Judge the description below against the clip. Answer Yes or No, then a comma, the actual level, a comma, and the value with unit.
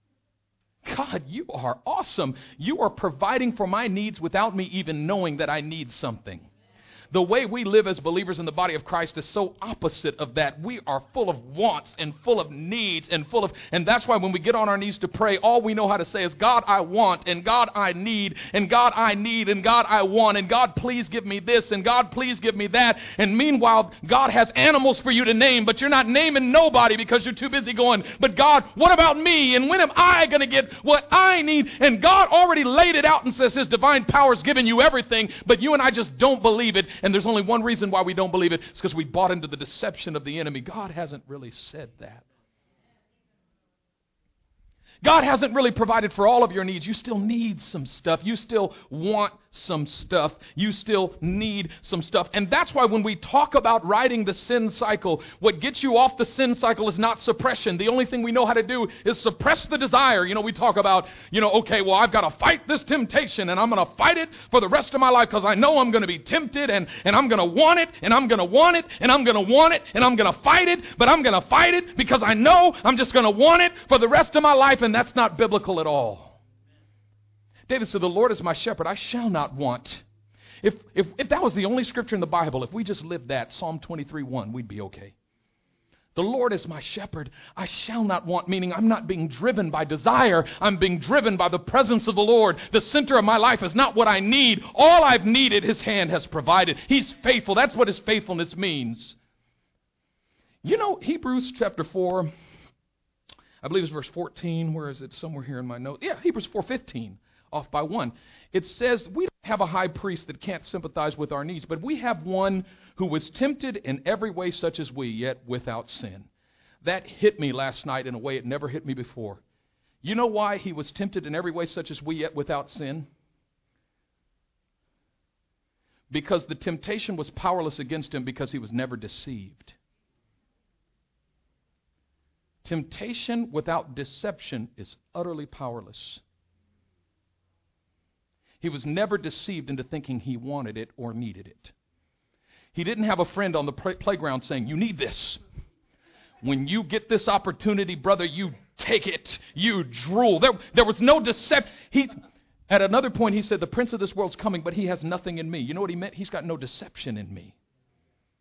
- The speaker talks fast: Yes, fast, 215 wpm